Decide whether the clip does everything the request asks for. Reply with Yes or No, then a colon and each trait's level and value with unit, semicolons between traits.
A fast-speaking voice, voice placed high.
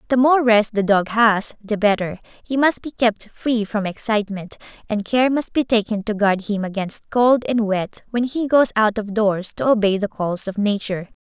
Yes: fast, 210 wpm; high, 215 Hz